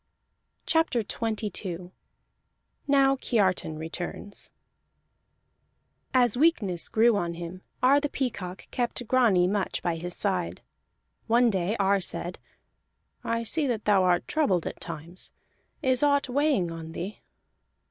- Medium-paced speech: No, slow, 120 wpm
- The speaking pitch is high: Yes, high, 205 Hz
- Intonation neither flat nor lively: No, wide, 6.0 semitones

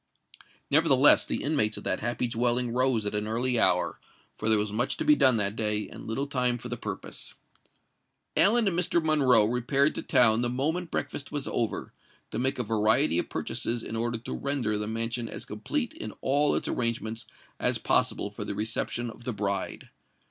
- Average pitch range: Yes, average, 3.9 semitones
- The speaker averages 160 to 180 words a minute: No, average, 190 wpm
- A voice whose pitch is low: Yes, low, 120 Hz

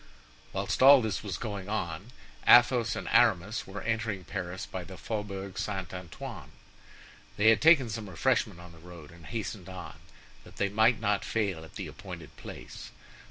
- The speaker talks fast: No, average, 165 wpm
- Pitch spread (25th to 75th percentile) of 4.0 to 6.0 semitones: No, average, 3.5 semitones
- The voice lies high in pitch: No, low, 100 Hz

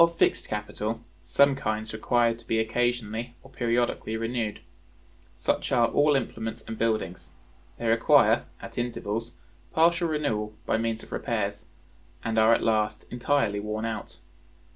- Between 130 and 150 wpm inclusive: Yes, average, 140 wpm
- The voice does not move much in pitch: Yes, narrow, 2.0 semitones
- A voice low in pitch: Yes, low, 115 Hz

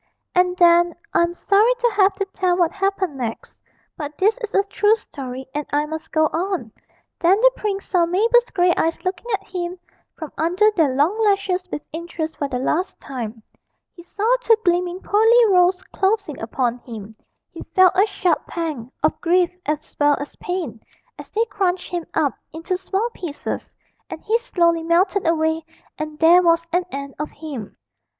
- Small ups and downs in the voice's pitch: No, average, 4.2 semitones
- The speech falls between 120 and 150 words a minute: No, average, 180 wpm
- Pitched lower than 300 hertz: No, very high, 350 Hz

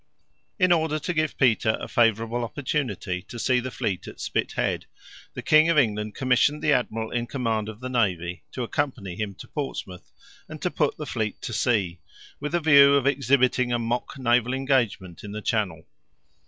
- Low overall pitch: Yes, low, 120 Hz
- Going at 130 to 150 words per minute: No, average, 180 wpm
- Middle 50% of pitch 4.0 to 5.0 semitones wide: Yes, average, 4.5 semitones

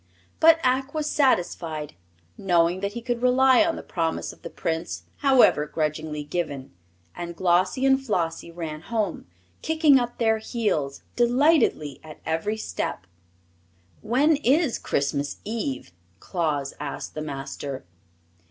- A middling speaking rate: No, slow, 130 wpm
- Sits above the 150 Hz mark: Yes, medium, 185 Hz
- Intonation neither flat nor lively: No, wide, 8.7 semitones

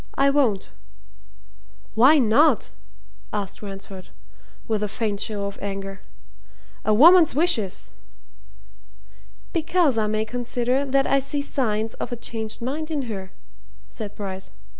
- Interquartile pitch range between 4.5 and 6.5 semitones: Yes, average, 5.1 semitones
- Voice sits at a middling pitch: No, high, 225 Hz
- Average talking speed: No, slow, 125 wpm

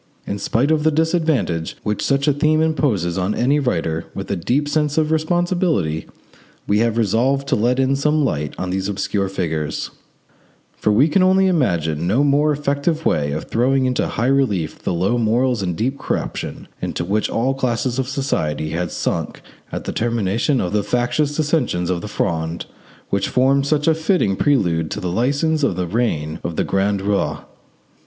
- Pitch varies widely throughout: Yes, wide, 7.7 semitones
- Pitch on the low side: Yes, low, 120 Hz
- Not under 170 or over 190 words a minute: Yes, average, 180 wpm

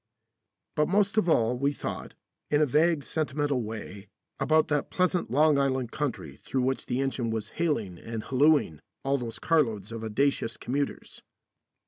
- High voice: No, low, 135 Hz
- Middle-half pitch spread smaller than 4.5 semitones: No, average, 4.9 semitones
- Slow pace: No, average, 155 wpm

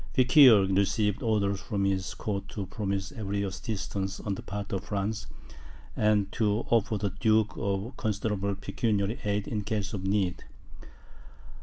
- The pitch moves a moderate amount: No, narrow, 1.8 semitones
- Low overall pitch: Yes, low, 100 Hz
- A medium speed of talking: Yes, average, 145 wpm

